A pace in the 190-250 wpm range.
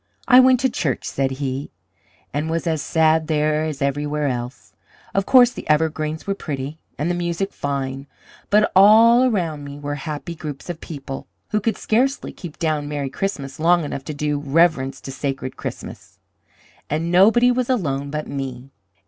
No: average, 170 wpm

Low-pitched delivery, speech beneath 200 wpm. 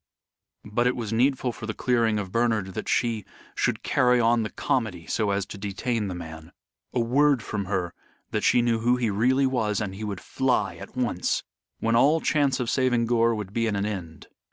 No: low, 115 Hz; fast, 205 wpm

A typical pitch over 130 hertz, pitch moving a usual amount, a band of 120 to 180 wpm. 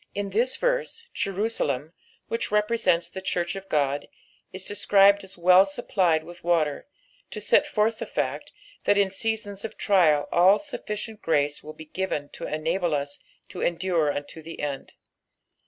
Yes: medium, 185 Hz; average, 4.5 semitones; average, 155 wpm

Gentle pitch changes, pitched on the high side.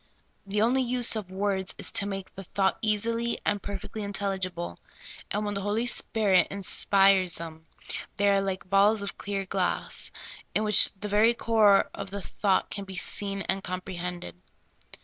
Yes: narrow, 1.7 semitones; high, 200 Hz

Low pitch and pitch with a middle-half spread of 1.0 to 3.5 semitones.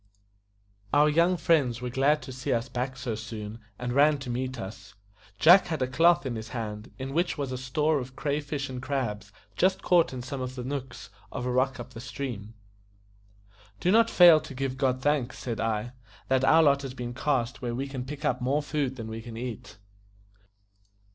Yes: low, 130 Hz; average, 3.1 semitones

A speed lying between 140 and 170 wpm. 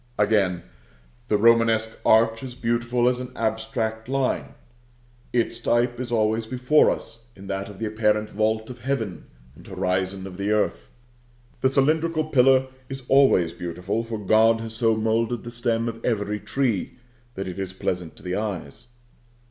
Yes: average, 160 wpm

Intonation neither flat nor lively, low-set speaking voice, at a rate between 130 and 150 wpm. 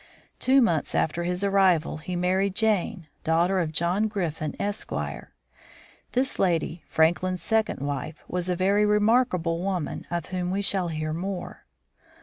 No: average, 3.1 semitones; medium, 180 Hz; average, 140 wpm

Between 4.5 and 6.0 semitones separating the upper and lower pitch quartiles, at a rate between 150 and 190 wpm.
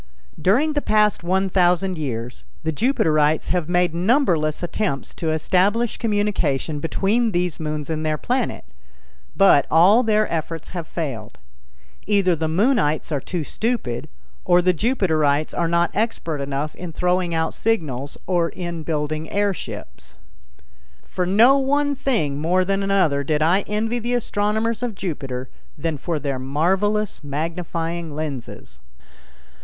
No: average, 5.1 semitones; average, 140 wpm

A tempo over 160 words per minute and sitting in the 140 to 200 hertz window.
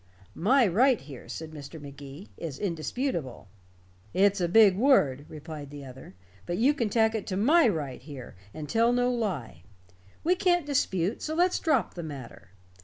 Yes: average, 170 wpm; medium, 185 Hz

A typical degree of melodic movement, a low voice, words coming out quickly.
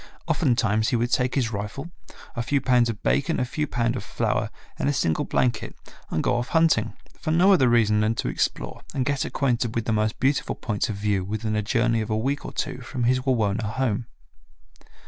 Yes: average, 3.5 semitones; low, 120 Hz; fast, 215 wpm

